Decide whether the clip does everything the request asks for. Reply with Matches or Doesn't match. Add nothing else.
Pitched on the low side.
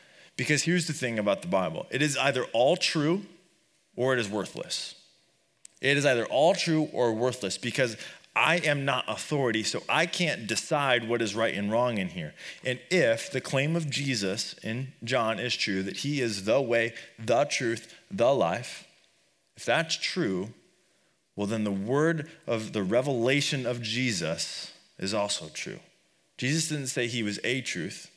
Matches